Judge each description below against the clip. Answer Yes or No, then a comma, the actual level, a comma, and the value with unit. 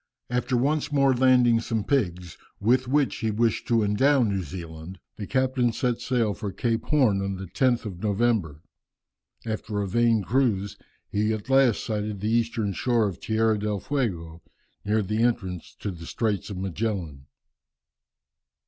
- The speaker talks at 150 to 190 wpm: Yes, average, 155 wpm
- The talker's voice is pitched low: Yes, low, 110 Hz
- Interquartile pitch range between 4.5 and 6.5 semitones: No, average, 3.8 semitones